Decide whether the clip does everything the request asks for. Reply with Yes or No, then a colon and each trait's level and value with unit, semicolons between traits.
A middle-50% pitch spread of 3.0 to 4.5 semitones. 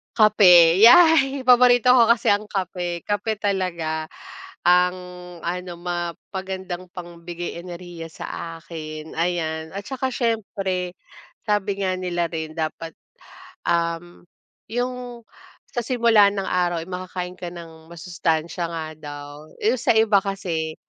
Yes: average, 3.6 semitones